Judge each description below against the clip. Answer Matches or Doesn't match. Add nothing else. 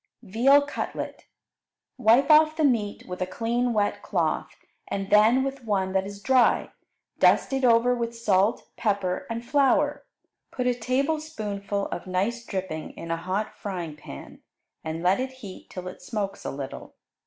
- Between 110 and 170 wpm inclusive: Matches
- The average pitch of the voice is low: Doesn't match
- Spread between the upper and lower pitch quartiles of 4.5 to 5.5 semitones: Matches